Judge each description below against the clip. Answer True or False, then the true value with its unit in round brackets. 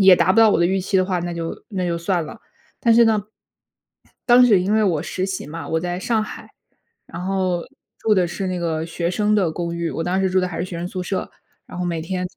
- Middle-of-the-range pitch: True (180 Hz)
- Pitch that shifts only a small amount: True (2.2 semitones)